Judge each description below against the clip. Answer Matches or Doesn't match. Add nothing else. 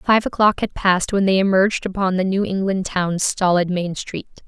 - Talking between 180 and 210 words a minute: Matches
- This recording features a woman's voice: Matches